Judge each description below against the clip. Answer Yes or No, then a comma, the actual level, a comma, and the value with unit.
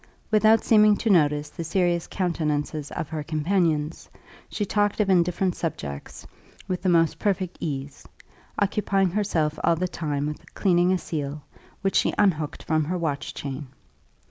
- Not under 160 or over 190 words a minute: No, average, 150 wpm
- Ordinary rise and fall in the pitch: Yes, average, 4.2 semitones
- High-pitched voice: No, medium, 170 Hz